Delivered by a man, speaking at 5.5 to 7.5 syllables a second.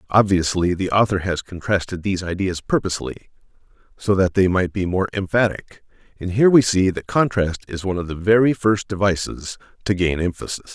Yes: male; 5.6 syllables/s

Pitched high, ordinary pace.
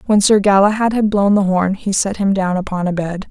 No: high, 195 Hz; fast, 255 wpm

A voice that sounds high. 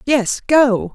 Yes: high, 245 Hz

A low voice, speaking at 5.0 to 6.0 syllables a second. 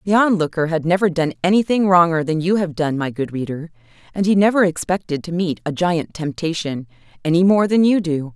No: medium, 170 Hz; 5.6 syllables/s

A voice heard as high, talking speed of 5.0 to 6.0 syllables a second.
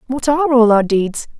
Yes: high, 245 Hz; 5.3 syllables/s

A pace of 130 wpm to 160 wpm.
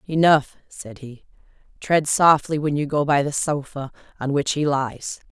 No: average, 170 wpm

